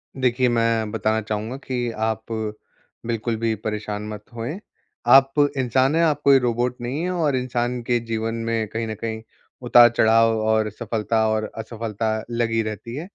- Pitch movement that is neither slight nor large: No, narrow, 2.1 semitones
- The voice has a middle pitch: No, low, 115 Hz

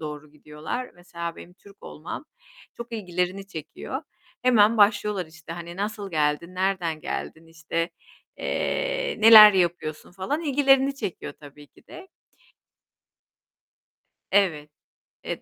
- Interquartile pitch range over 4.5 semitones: Yes, average, 4.9 semitones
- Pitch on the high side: No, medium, 180 Hz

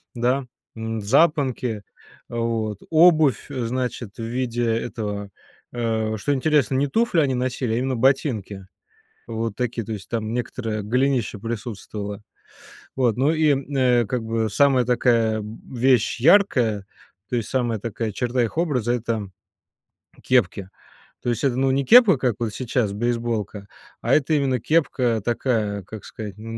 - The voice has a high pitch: No, low, 120 Hz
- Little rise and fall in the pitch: No, average, 3.2 semitones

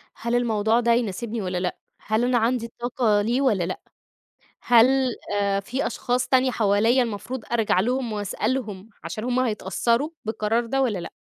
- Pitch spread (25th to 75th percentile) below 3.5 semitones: Yes, average, 3.0 semitones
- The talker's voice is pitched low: No, high, 230 Hz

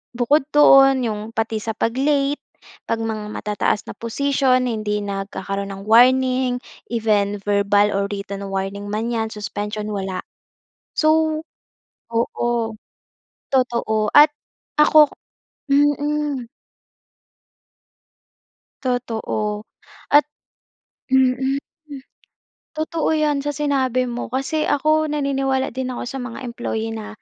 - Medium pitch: No, high, 240 Hz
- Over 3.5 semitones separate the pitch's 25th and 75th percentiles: Yes, average, 4.6 semitones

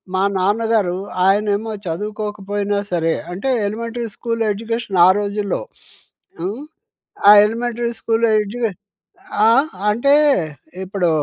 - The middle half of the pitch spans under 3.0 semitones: Yes, narrow, 2.5 semitones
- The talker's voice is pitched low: No, high, 210 Hz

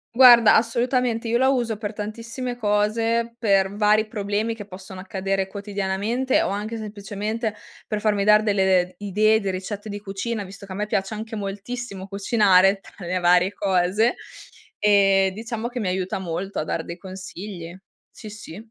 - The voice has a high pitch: Yes, high, 205 Hz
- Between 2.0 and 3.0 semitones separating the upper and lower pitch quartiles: Yes, narrow, 2.5 semitones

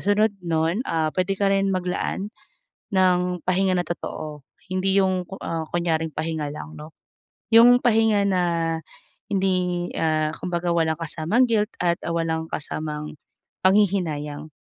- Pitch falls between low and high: Yes, medium, 180 Hz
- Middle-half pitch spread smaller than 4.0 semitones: Yes, average, 3.4 semitones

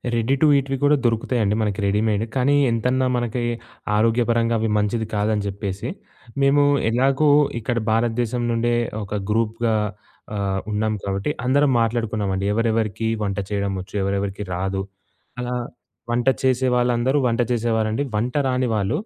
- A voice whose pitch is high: No, low, 115 Hz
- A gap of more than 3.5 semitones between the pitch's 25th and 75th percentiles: No, average, 2.9 semitones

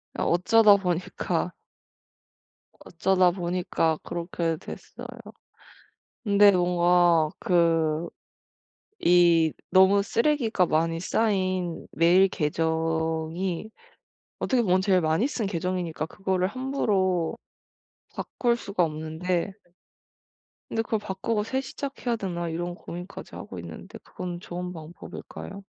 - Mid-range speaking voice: Yes, medium, 180 Hz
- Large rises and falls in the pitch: No, average, 3.0 semitones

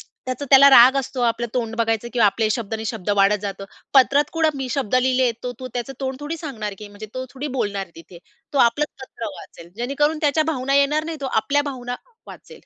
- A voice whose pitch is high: Yes, very high, 255 Hz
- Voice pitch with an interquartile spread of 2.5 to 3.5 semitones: No, average, 3.9 semitones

